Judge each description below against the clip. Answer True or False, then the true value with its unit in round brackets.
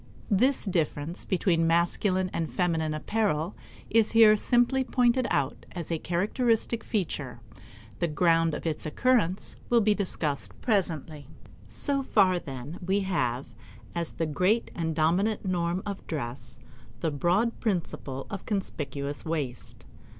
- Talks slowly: True (130 wpm)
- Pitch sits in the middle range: True (175 Hz)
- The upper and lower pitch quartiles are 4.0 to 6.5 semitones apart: True (5.1 semitones)